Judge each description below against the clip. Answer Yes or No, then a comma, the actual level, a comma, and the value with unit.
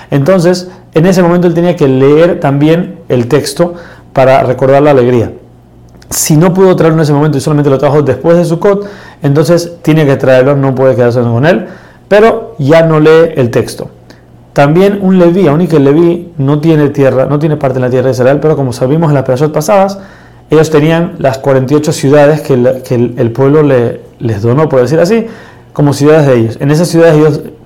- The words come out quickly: Yes, fast, 205 wpm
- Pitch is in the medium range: Yes, medium, 150 Hz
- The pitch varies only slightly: No, average, 4.2 semitones